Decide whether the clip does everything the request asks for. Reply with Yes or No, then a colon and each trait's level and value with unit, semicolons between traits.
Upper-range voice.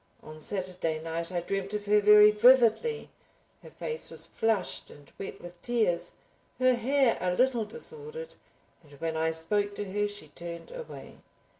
Yes: high, 205 Hz